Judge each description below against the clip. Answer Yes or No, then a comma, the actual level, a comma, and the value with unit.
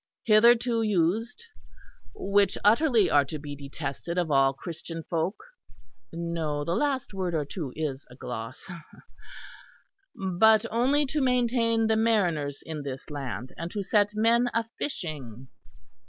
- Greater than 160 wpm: No, slow, 135 wpm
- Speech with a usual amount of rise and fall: No, wide, 7.6 semitones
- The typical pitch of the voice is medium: Yes, medium, 180 Hz